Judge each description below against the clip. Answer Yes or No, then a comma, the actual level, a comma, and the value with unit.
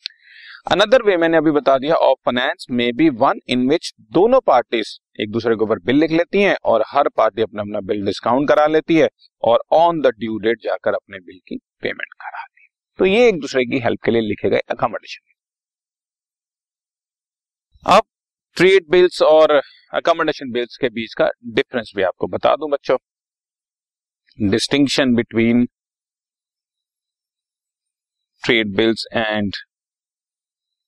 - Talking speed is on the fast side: No, average, 150 wpm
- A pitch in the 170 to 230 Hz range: No, low, 135 Hz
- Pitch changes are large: Yes, wide, 6.6 semitones